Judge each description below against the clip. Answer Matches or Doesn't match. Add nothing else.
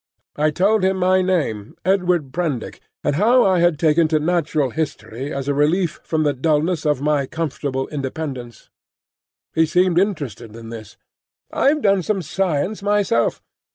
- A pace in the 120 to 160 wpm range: Matches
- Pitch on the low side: Doesn't match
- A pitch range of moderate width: Matches